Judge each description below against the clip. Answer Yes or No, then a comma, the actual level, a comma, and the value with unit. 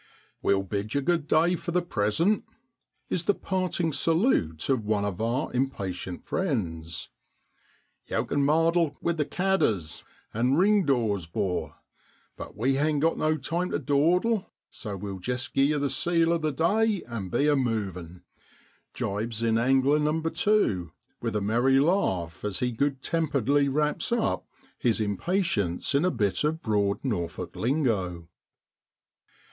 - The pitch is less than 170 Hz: Yes, low, 135 Hz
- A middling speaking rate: Yes, average, 160 wpm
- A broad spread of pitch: Yes, wide, 7.9 semitones